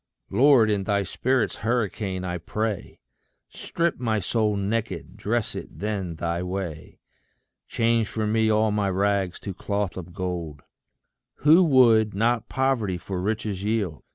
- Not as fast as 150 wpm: Yes, average, 140 wpm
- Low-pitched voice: Yes, low, 105 Hz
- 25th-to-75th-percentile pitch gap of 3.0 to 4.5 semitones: Yes, average, 3.5 semitones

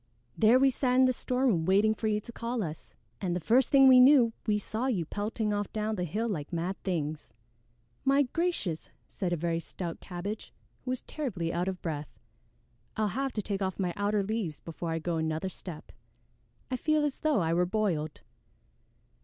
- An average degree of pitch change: No, wide, 6.1 semitones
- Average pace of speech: Yes, average, 195 wpm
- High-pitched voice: Yes, high, 205 Hz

